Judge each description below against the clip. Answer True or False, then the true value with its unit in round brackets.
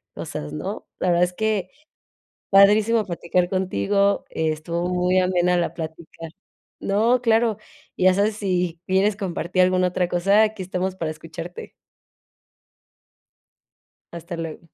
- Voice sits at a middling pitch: True (180 Hz)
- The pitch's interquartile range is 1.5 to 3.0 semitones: True (2.6 semitones)